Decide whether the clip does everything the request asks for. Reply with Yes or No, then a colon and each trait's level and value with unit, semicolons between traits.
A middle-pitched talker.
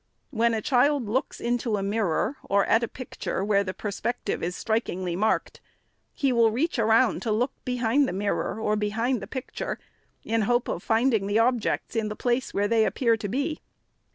No: high, 225 Hz